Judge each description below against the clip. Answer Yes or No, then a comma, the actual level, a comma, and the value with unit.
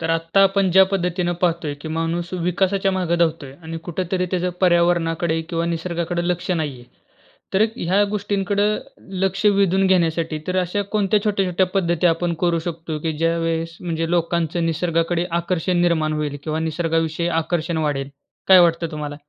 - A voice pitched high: No, medium, 170 Hz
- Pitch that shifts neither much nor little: No, narrow, 1.9 semitones